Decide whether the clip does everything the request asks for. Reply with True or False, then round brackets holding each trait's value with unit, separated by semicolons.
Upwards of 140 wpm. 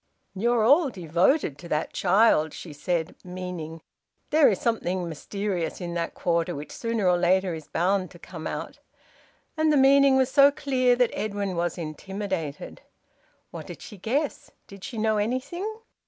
True (165 wpm)